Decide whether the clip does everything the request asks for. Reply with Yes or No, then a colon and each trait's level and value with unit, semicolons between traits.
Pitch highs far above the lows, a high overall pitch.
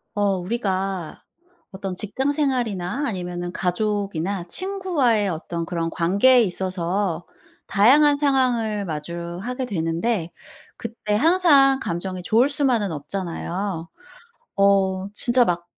Yes: wide, 5.7 semitones; high, 200 Hz